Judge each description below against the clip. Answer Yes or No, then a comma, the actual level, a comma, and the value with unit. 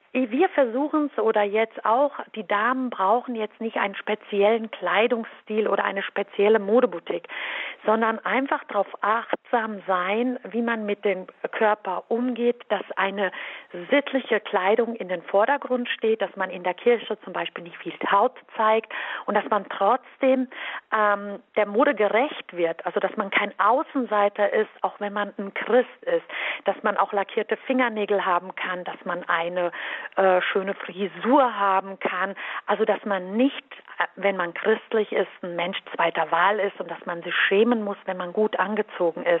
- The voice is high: Yes, high, 210 Hz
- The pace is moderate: Yes, average, 165 wpm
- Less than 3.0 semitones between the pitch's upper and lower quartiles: No, average, 3.4 semitones